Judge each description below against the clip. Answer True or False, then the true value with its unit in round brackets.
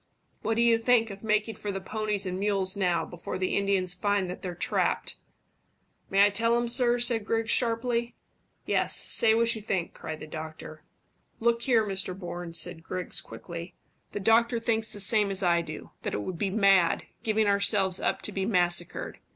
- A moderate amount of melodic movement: True (3.7 semitones)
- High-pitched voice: True (200 Hz)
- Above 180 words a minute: True (190 wpm)